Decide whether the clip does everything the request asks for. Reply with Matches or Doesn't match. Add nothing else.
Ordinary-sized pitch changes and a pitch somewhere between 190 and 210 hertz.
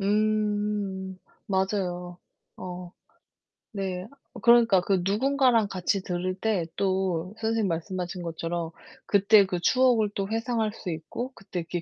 Matches